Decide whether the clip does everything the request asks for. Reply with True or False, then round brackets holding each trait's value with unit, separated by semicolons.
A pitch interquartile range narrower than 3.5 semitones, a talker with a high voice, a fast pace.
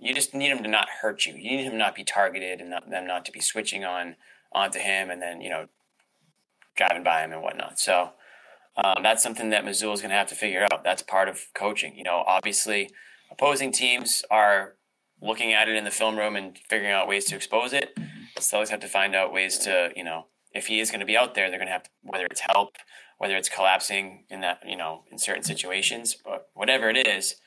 False (2.8 semitones; 100 Hz; 240 wpm)